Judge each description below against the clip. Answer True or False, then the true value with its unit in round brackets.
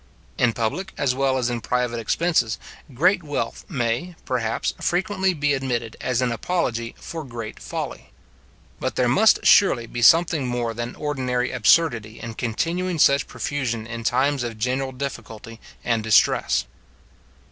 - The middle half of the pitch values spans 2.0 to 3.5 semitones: False (4.0 semitones)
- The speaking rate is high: False (145 wpm)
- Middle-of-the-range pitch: False (125 Hz)